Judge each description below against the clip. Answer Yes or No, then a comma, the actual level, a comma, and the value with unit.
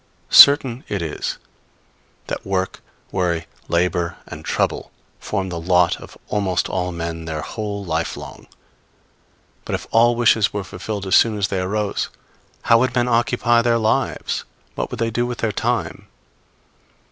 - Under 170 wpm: Yes, average, 155 wpm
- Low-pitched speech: Yes, low, 100 Hz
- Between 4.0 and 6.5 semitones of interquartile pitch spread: Yes, average, 4.5 semitones